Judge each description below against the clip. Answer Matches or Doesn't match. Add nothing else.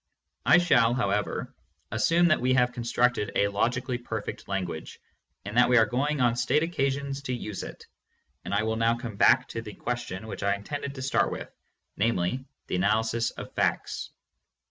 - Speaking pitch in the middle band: Doesn't match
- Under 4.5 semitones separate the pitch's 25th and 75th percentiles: Matches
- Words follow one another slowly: Doesn't match